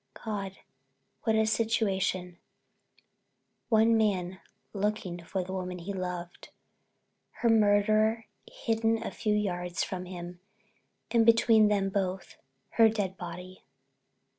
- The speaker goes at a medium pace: No, slow, 110 wpm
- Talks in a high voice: Yes, high, 200 Hz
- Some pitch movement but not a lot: Yes, average, 3.2 semitones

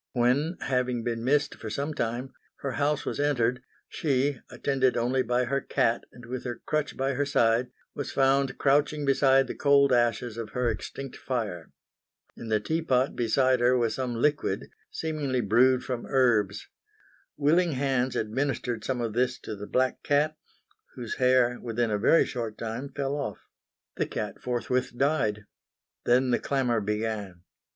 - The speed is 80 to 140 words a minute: No, average, 160 wpm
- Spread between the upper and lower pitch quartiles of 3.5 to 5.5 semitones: No, average, 2.9 semitones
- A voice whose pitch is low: Yes, low, 125 Hz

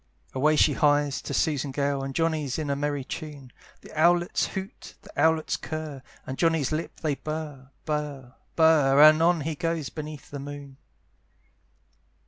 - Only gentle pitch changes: Yes, narrow, 2.2 semitones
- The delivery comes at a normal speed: Yes, average, 155 wpm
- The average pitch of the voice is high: No, medium, 150 Hz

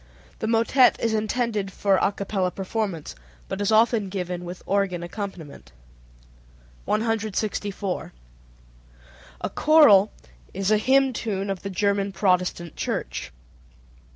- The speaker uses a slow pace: Yes, slow, 115 wpm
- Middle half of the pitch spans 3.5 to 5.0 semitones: No, average, 2.9 semitones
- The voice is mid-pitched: No, high, 200 Hz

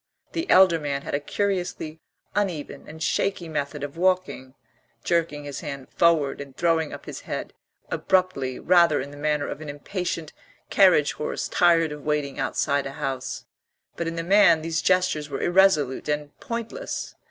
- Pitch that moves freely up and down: No, average, 3.8 semitones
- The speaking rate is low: No, average, 165 wpm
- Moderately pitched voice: Yes, medium, 155 Hz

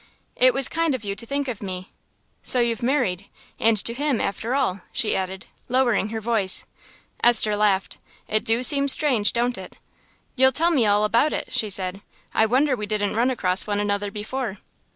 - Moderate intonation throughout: Yes, average, 4.0 semitones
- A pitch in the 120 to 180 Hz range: No, high, 225 Hz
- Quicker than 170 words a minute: Yes, average, 190 wpm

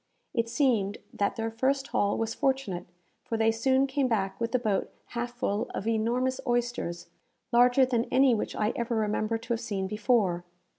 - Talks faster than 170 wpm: Yes, average, 180 wpm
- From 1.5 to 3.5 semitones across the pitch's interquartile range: Yes, average, 2.8 semitones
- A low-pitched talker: No, high, 230 Hz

